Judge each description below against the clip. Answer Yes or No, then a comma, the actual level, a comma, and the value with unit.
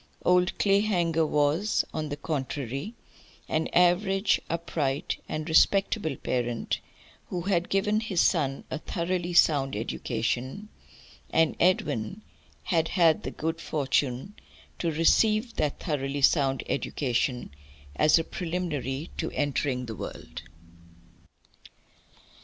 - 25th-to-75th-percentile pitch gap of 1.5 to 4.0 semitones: No, average, 4.7 semitones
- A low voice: No, medium, 160 Hz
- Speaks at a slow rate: Yes, slow, 110 wpm